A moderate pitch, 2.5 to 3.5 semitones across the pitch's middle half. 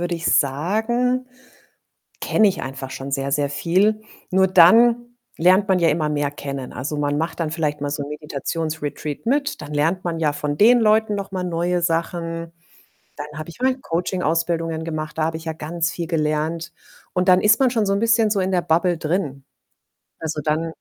No: medium, 165 Hz; average, 3.9 semitones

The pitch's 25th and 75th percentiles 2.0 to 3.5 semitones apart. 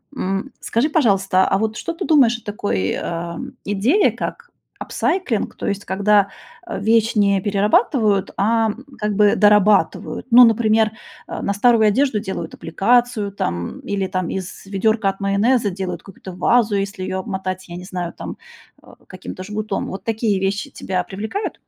Yes: average, 2.8 semitones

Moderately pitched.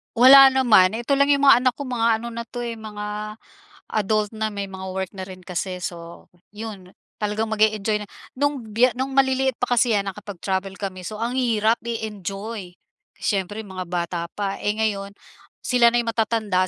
No: high, 215 Hz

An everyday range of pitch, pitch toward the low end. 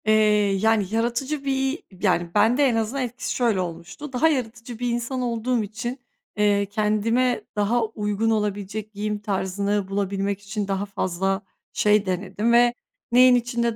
No: average, 3.1 semitones; high, 215 Hz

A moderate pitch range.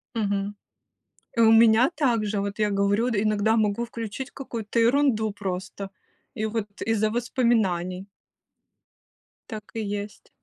No: narrow, 2.3 semitones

